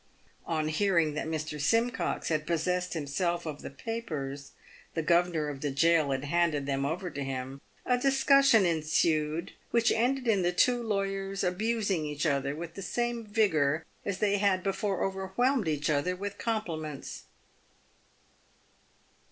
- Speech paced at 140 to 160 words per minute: Yes, average, 150 wpm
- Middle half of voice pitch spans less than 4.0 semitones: No, average, 5.0 semitones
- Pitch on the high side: No, medium, 175 Hz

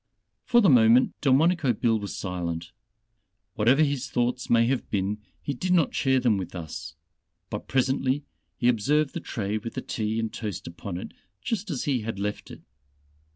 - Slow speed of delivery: No, average, 175 wpm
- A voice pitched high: No, low, 120 Hz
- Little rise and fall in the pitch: No, average, 4.9 semitones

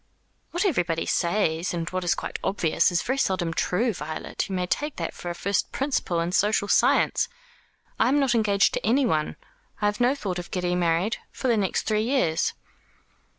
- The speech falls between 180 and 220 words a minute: Yes, average, 190 wpm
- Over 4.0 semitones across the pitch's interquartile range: Yes, wide, 5.5 semitones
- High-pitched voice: Yes, high, 195 Hz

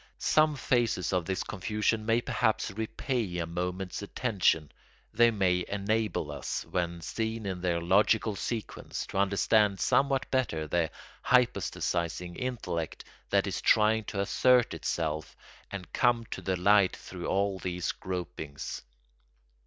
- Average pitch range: Yes, average, 4.2 semitones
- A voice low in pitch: Yes, low, 100 Hz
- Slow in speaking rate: Yes, slow, 130 wpm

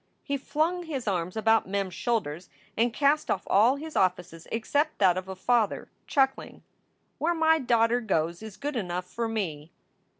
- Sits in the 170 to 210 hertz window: No, high, 225 Hz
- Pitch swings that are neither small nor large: No, wide, 7.0 semitones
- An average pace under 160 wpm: No, average, 170 wpm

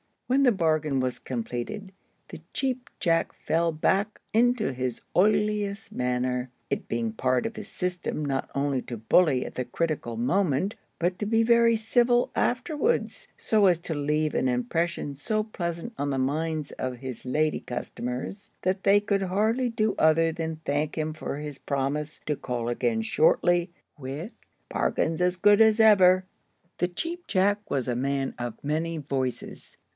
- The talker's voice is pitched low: No, medium, 165 Hz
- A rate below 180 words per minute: Yes, average, 160 wpm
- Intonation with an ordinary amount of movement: No, wide, 7.3 semitones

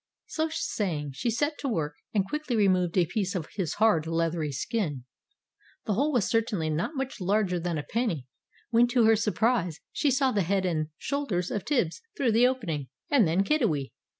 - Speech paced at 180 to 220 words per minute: Yes, average, 185 wpm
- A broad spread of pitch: Yes, wide, 6.5 semitones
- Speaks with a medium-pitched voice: No, high, 200 Hz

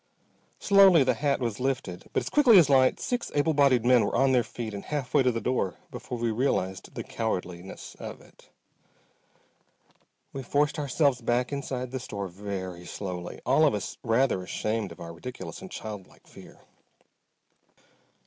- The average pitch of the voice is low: Yes, low, 125 Hz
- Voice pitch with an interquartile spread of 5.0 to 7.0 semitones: Yes, wide, 5.4 semitones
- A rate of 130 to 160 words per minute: No, average, 170 wpm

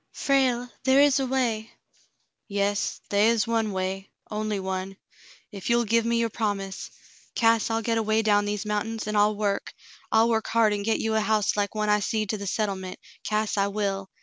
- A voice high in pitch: Yes, high, 215 Hz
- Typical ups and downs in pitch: No, narrow, 2.0 semitones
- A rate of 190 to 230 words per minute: Yes, fast, 205 wpm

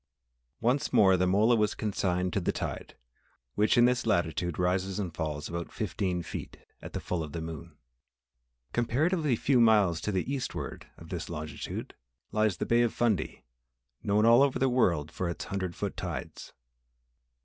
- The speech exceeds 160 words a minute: Yes, average, 170 wpm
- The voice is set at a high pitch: No, low, 100 Hz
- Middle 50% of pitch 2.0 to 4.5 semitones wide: No, wide, 5.4 semitones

